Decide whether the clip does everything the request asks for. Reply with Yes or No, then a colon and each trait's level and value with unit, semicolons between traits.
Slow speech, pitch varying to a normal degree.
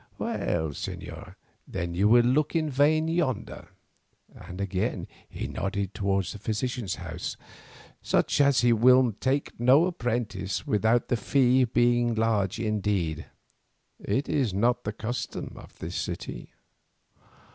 Yes: slow, 130 wpm; average, 4.4 semitones